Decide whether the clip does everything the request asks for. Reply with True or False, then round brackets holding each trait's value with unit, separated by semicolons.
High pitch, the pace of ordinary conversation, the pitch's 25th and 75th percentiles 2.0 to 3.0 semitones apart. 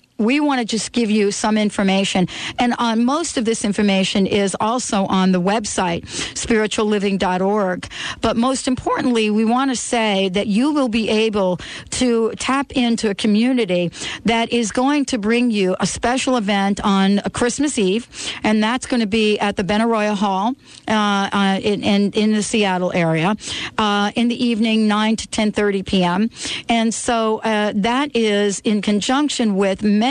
True (215 Hz; 165 wpm; 2.7 semitones)